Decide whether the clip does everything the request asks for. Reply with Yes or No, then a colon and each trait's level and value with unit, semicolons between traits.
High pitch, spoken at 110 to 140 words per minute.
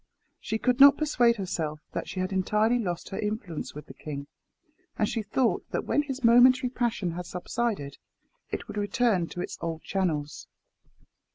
No: high, 210 Hz; average, 170 wpm